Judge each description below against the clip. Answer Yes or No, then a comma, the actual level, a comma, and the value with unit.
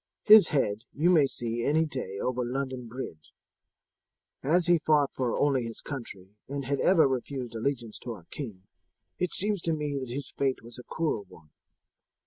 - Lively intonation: No, average, 4.1 semitones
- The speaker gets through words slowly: No, average, 175 wpm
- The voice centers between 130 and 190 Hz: Yes, low, 135 Hz